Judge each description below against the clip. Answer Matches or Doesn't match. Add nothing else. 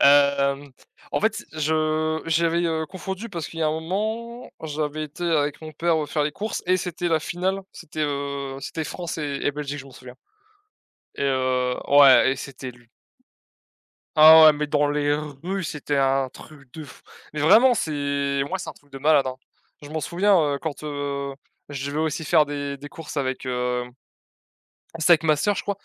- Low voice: Doesn't match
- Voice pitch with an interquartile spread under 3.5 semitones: Matches